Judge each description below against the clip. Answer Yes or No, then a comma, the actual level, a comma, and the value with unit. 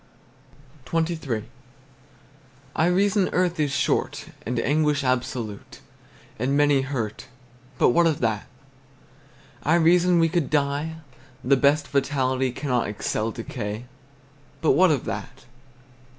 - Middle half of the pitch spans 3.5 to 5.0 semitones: Yes, average, 4.4 semitones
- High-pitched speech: No, medium, 140 Hz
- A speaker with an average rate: No, slow, 115 wpm